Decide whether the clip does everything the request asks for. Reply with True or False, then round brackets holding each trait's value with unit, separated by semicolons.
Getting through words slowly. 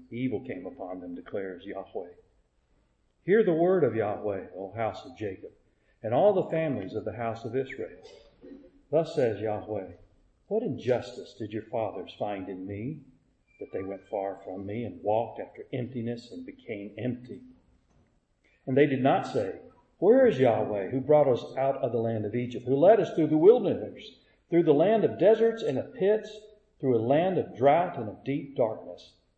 False (180 wpm)